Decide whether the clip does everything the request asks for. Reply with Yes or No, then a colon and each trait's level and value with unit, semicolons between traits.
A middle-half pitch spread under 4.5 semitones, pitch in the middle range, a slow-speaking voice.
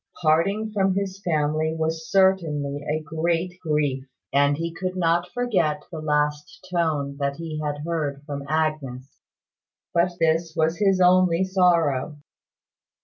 Yes: average, 3.3 semitones; medium, 160 Hz; slow, 130 wpm